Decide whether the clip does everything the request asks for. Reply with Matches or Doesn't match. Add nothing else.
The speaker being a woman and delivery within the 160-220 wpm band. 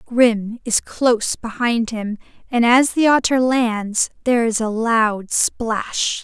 Doesn't match